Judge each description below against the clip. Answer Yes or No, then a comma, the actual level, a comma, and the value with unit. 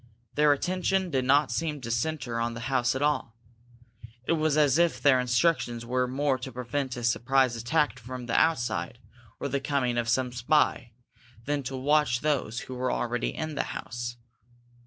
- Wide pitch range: No, average, 3.6 semitones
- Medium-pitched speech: No, low, 130 Hz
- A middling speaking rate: Yes, average, 175 wpm